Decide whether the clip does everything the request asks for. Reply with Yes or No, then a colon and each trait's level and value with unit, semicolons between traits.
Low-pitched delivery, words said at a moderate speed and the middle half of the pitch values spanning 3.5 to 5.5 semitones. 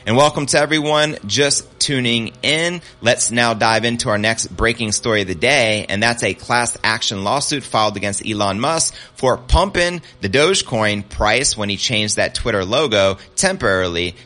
Yes: low, 115 Hz; average, 170 wpm; average, 4.5 semitones